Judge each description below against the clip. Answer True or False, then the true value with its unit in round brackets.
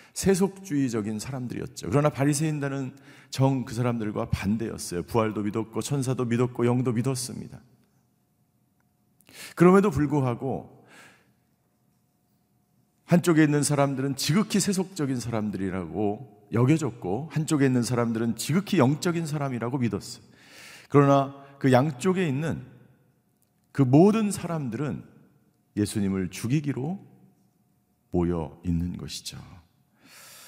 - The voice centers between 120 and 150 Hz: True (135 Hz)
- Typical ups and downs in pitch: True (4.8 semitones)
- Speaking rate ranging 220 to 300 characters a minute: True (275 characters per minute)